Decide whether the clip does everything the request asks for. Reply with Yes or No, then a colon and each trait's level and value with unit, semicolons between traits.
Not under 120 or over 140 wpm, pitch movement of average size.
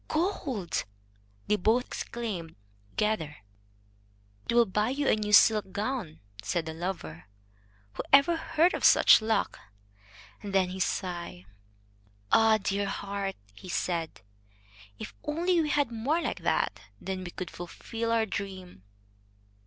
Yes: slow, 135 wpm; average, 4.6 semitones